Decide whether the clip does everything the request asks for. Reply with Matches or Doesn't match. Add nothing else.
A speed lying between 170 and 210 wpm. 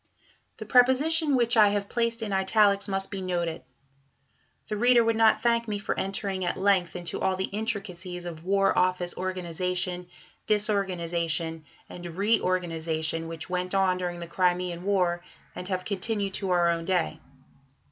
Doesn't match